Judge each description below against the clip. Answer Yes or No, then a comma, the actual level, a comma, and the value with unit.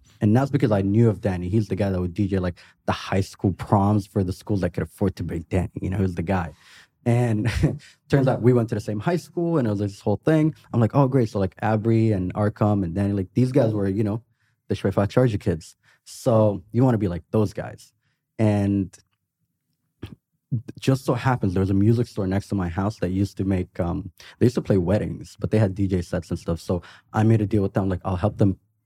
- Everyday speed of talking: No, fast, 250 wpm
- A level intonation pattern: No, average, 3.3 semitones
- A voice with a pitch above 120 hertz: No, low, 105 Hz